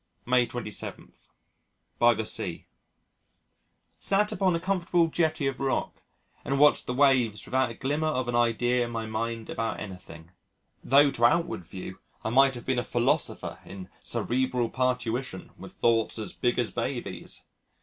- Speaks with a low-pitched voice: Yes, low, 125 Hz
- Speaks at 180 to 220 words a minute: No, average, 155 wpm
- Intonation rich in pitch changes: No, average, 3.2 semitones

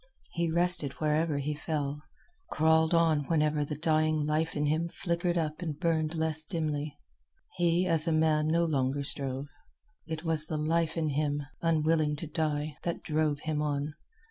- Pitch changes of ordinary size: No, narrow, 1.7 semitones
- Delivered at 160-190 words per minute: Yes, average, 165 wpm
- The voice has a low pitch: No, medium, 155 Hz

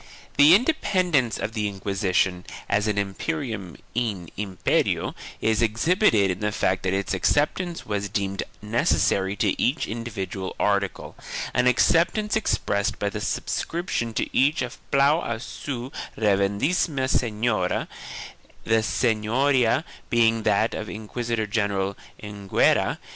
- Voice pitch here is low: Yes, low, 110 Hz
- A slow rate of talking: Yes, slow, 125 wpm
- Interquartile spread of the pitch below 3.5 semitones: No, average, 4.5 semitones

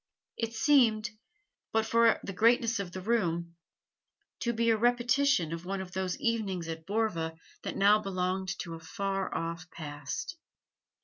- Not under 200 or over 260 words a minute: No, average, 150 wpm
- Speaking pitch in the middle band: No, high, 195 Hz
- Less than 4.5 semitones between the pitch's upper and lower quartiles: No, average, 4.9 semitones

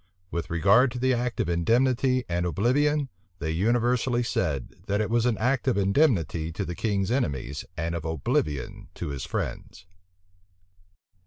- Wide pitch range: Yes, wide, 6.9 semitones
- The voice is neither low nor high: No, low, 100 Hz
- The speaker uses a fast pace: No, average, 155 wpm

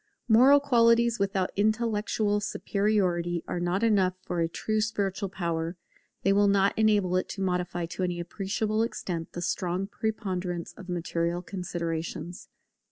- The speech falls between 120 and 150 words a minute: Yes, average, 140 wpm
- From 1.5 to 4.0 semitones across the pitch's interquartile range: Yes, average, 3.4 semitones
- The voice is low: No, high, 190 Hz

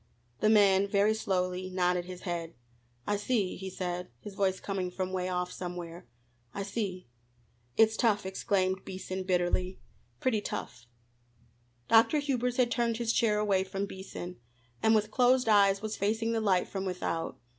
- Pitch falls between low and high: No, high, 195 Hz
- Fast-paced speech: No, average, 155 wpm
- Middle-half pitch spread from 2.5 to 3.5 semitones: Yes, average, 3.0 semitones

